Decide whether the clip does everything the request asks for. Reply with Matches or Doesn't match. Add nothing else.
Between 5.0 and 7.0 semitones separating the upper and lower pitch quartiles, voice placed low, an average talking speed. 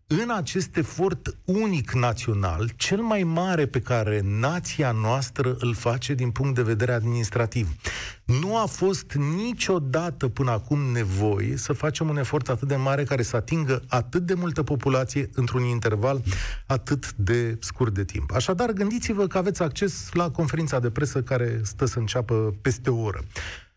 Matches